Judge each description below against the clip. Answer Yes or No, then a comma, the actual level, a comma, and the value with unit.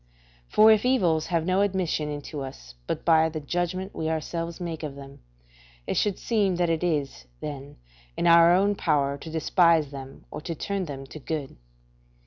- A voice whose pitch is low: No, medium, 165 Hz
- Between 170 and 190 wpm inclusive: Yes, average, 180 wpm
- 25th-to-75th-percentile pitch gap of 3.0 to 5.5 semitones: Yes, average, 3.5 semitones